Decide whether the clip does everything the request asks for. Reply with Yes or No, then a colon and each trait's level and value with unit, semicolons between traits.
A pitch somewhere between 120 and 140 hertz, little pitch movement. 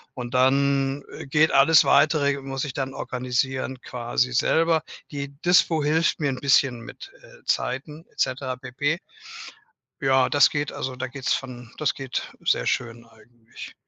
Yes: low, 135 Hz; narrow, 2.2 semitones